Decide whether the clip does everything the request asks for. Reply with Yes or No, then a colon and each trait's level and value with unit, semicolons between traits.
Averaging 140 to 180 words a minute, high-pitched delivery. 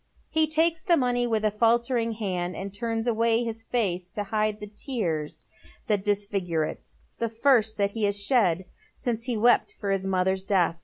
No: average, 190 wpm; high, 215 Hz